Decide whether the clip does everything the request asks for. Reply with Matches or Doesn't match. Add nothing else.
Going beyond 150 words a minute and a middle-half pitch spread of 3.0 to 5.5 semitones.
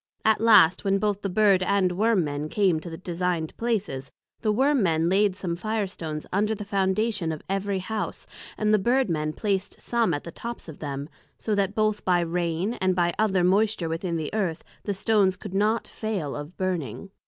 Matches